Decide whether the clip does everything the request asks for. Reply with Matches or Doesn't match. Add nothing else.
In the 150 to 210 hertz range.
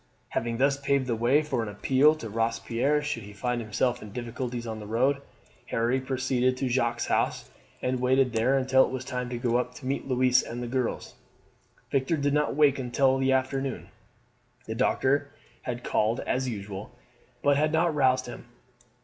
Doesn't match